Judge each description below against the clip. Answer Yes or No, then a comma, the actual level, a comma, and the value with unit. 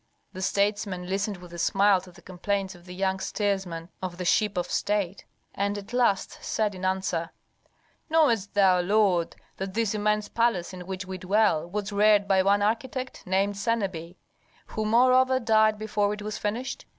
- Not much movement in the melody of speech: Yes, narrow, 2.3 semitones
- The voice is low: No, high, 200 Hz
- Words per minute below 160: No, average, 175 wpm